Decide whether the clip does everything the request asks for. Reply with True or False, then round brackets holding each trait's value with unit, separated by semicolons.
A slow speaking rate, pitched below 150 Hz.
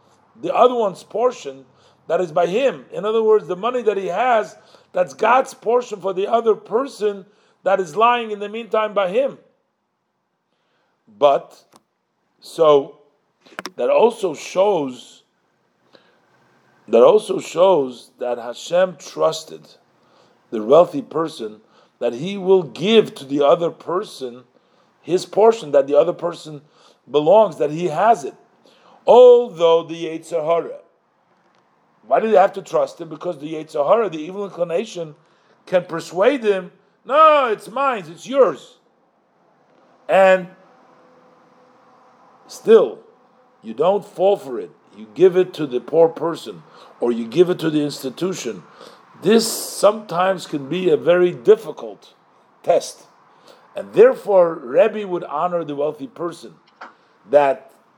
False (130 wpm; 185 Hz)